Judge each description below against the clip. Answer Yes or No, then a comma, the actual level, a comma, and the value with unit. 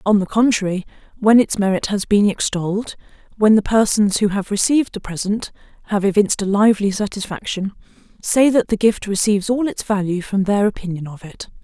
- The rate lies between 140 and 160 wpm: No, average, 180 wpm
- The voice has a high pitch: Yes, high, 205 Hz